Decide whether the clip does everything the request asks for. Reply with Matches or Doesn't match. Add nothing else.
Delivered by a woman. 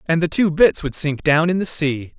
Doesn't match